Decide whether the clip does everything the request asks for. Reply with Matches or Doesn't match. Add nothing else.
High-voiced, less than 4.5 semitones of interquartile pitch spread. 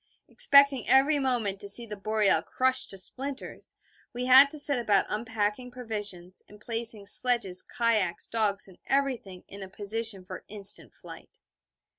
Matches